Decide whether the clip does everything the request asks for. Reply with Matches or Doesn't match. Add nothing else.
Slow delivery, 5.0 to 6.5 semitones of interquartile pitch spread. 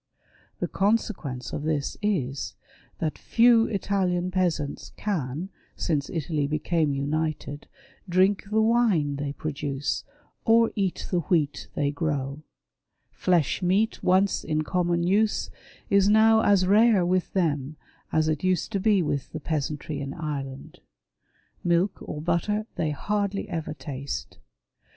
Matches